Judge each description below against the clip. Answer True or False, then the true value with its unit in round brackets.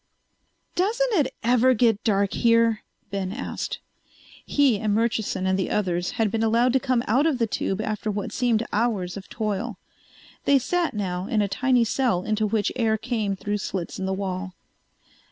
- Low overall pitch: False (220 Hz)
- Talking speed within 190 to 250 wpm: False (175 wpm)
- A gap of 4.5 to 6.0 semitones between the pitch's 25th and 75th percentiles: False (3.5 semitones)